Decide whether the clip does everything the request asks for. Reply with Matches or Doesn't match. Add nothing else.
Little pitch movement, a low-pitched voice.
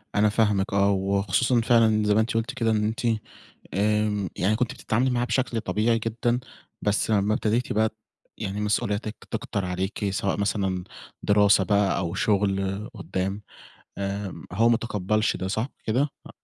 Matches